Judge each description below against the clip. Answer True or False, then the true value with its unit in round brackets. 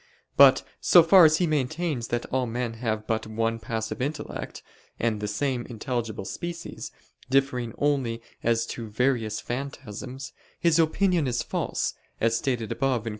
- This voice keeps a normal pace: True (150 wpm)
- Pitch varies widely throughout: False (3.8 semitones)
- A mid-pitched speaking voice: False (125 Hz)